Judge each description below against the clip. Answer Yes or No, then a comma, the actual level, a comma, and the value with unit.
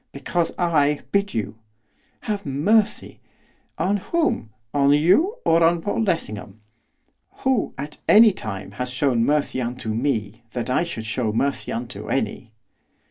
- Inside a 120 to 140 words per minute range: Yes, slow, 135 wpm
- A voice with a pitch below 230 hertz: Yes, medium, 140 Hz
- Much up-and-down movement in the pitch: Yes, wide, 7.9 semitones